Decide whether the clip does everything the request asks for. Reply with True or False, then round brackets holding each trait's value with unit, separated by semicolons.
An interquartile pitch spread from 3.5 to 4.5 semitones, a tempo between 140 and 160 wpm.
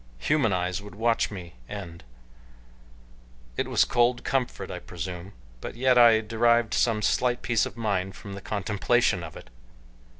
True (4.2 semitones; 155 wpm)